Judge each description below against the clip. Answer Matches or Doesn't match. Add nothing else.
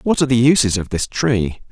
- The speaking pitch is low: Matches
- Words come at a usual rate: Doesn't match